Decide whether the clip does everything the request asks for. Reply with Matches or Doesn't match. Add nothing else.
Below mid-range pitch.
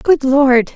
Doesn't match